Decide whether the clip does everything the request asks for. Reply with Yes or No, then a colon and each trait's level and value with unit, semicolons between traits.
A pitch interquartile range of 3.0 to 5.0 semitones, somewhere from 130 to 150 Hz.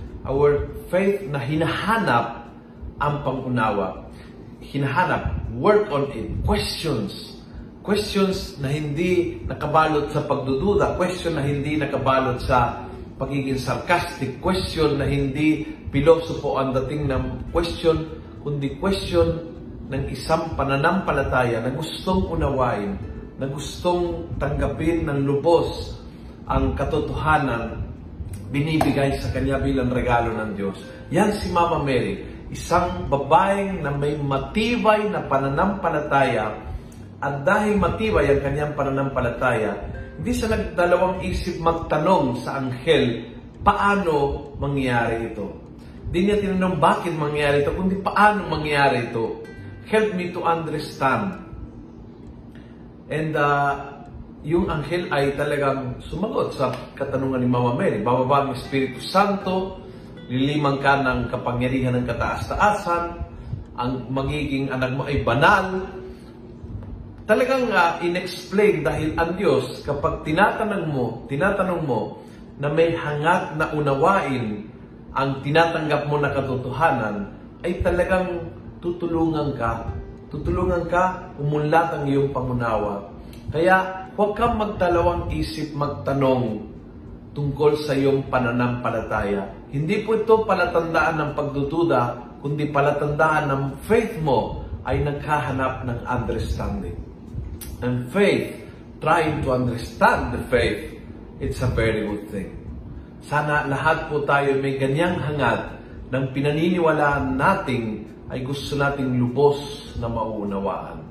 No: wide, 5.4 semitones; medium, 140 Hz